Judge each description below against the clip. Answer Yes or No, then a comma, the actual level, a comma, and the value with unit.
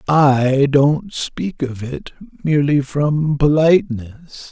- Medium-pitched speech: Yes, medium, 145 Hz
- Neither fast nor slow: No, slow, 105 wpm